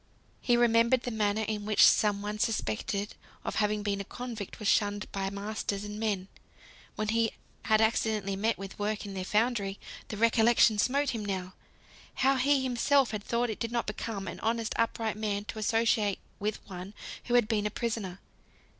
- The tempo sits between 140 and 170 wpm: No, average, 185 wpm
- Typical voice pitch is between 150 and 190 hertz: No, high, 215 Hz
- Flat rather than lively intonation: Yes, narrow, 2.2 semitones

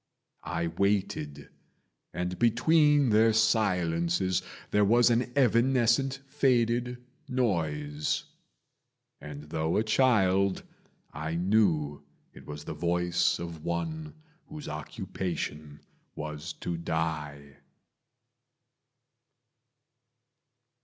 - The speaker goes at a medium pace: No, slow, 85 wpm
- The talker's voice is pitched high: No, very low, 90 Hz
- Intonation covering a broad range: Yes, wide, 7.0 semitones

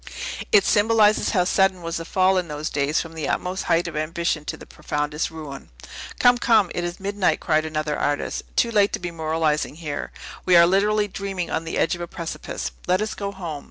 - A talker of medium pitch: Yes, medium, 175 Hz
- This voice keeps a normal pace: No, fast, 210 wpm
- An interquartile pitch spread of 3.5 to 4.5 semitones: Yes, average, 3.8 semitones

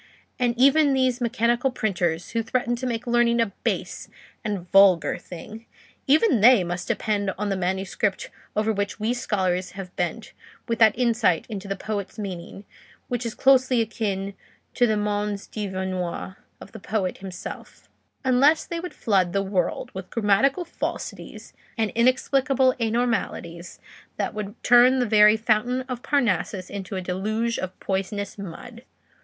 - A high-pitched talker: Yes, high, 215 Hz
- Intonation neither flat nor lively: Yes, average, 4.0 semitones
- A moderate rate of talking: Yes, average, 150 wpm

